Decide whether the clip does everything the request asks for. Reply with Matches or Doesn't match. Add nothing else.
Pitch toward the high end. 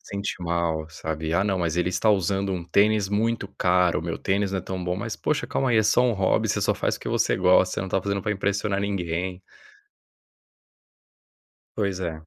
Doesn't match